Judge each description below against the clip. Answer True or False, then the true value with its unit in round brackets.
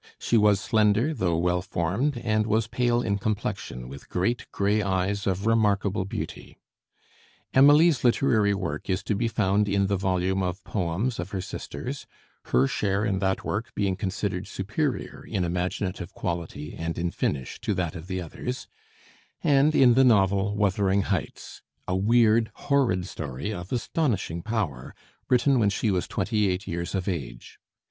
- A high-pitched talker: False (100 Hz)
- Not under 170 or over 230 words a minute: False (160 wpm)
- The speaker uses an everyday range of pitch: True (3.6 semitones)